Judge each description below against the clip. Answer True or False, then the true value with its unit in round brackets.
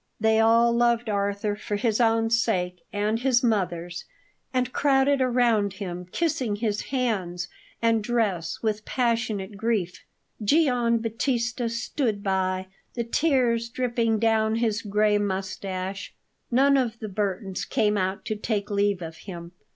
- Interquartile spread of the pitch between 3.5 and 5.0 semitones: False (2.9 semitones)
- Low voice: False (220 Hz)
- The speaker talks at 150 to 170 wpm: False (135 wpm)